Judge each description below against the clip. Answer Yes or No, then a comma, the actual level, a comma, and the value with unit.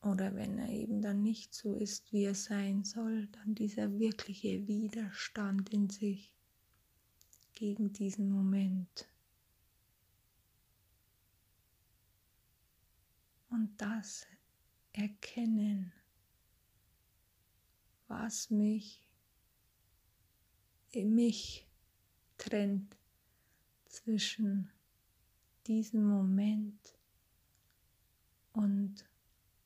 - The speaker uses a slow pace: Yes, slow, 65 wpm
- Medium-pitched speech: No, high, 195 Hz